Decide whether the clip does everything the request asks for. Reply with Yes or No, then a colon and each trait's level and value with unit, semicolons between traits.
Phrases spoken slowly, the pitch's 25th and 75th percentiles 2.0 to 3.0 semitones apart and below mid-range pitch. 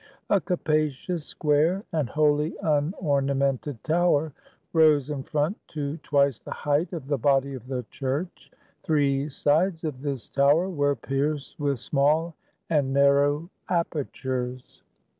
No: slow, 125 wpm; narrow, 2.4 semitones; medium, 145 Hz